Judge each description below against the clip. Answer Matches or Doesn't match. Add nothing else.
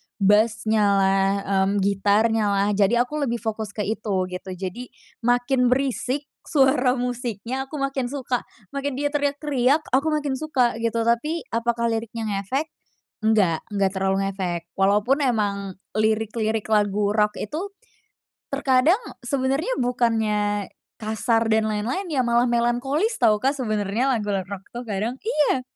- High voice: Matches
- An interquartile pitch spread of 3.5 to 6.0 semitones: Matches